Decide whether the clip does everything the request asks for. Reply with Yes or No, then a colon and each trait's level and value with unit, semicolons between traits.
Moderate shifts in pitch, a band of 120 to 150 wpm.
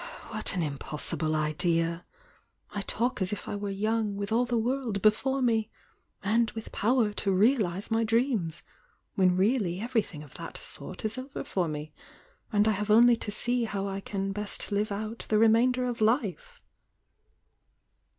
No: average, 3.3 semitones; average, 165 wpm